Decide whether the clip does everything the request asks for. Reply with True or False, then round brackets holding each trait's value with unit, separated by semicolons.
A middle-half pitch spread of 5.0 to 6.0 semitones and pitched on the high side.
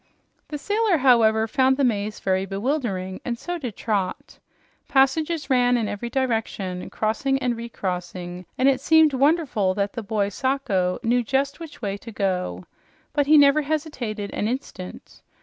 True (5.6 semitones; 240 Hz)